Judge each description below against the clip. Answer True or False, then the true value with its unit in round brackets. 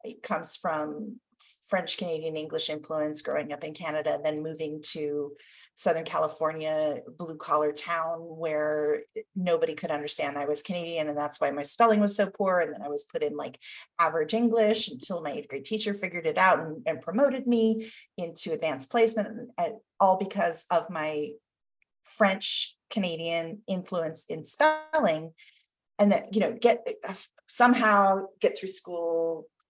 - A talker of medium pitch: True (170 Hz)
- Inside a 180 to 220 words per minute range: False (160 wpm)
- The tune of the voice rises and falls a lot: True (5.9 semitones)